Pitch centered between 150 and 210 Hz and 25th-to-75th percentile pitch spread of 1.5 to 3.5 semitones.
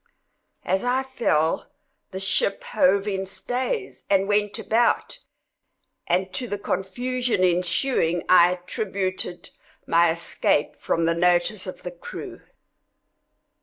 No: high, 190 Hz; wide, 5.6 semitones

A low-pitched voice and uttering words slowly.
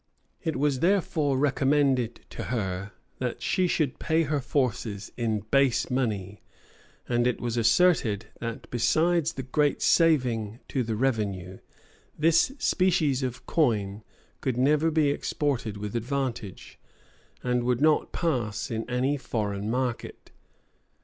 Yes: low, 125 Hz; slow, 130 wpm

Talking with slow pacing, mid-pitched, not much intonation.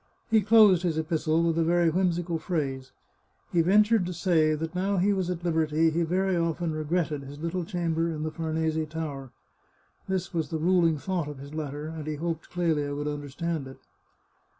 No: average, 185 wpm; medium, 165 Hz; narrow, 2.3 semitones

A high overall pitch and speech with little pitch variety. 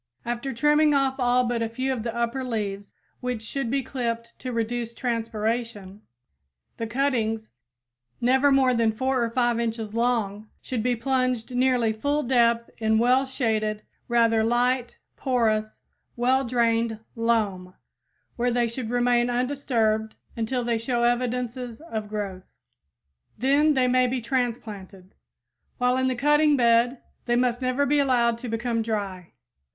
Yes: high, 240 Hz; narrow, 2.1 semitones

